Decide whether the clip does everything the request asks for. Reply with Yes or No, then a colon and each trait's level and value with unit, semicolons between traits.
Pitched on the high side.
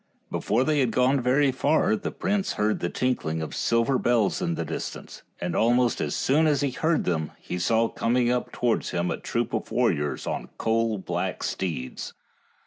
No: low, 120 Hz